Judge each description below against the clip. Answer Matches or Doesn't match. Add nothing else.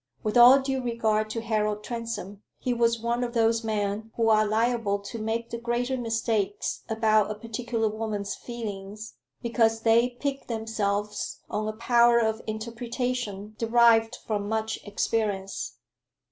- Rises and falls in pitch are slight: Matches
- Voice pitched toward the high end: Matches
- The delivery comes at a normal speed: Matches